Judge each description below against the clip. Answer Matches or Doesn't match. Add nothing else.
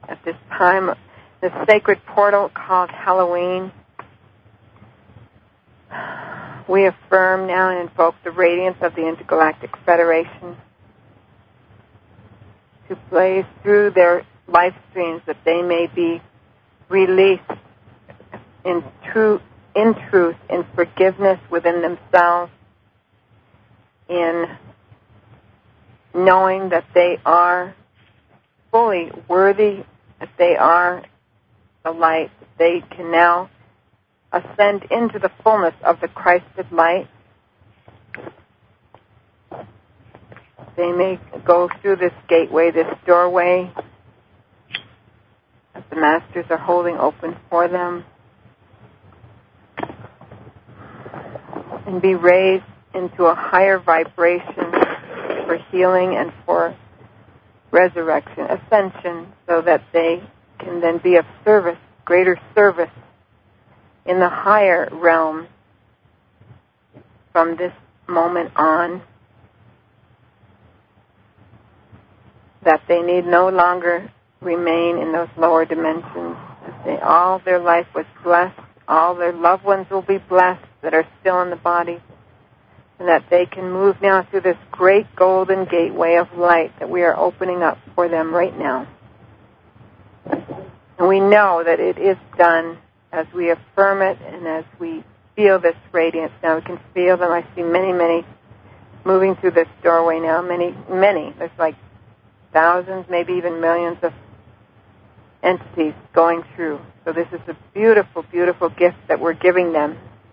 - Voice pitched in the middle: Matches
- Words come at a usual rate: Doesn't match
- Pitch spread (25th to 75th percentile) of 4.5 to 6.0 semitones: Doesn't match